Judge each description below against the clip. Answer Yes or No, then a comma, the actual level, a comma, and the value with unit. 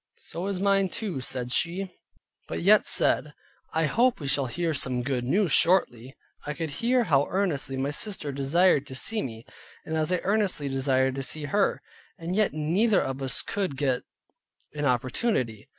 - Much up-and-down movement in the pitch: Yes, wide, 6.3 semitones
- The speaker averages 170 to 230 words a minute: Yes, average, 175 wpm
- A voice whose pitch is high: No, medium, 150 Hz